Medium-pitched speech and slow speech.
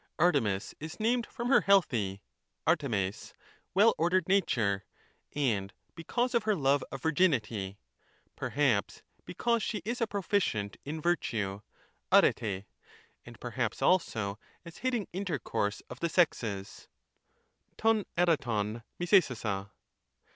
Yes: medium, 150 Hz; slow, 110 wpm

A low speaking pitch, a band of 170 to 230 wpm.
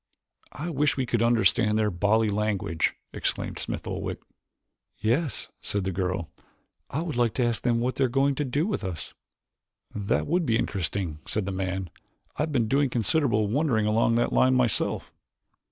Yes: low, 115 Hz; average, 175 wpm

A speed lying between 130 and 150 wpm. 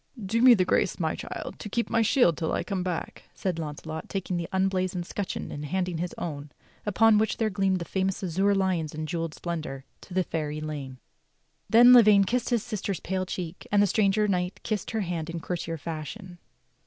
No: average, 200 wpm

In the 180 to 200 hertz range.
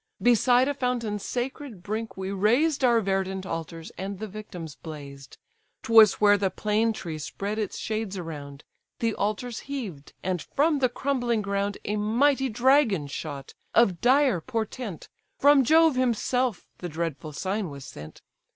No: high, 210 Hz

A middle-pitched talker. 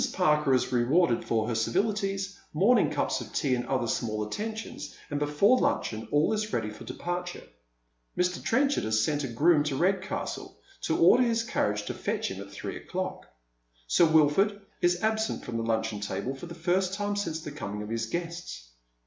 Yes: medium, 150 Hz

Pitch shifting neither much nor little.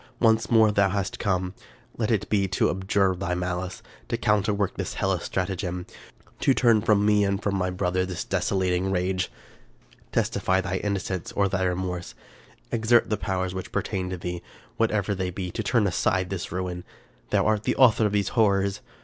No: narrow, 2.3 semitones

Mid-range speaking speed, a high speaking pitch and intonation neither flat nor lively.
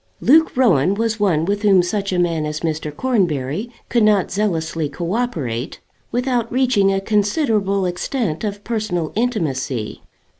No: average, 145 wpm; high, 195 Hz; wide, 5.8 semitones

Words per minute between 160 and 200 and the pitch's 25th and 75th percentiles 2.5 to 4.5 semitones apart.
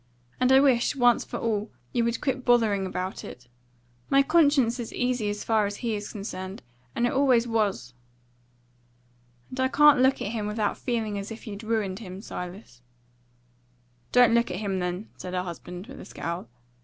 Yes: average, 180 wpm; average, 4.1 semitones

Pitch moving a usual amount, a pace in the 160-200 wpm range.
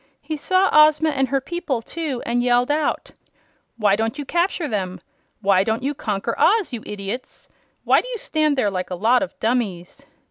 No: wide, 6.2 semitones; average, 185 wpm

